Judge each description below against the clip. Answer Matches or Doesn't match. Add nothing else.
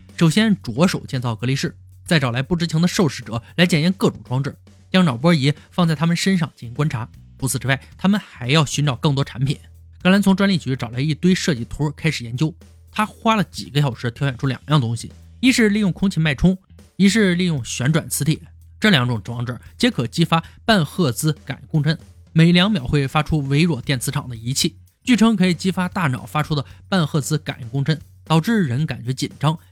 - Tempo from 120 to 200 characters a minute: Doesn't match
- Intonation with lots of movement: Matches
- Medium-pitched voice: Matches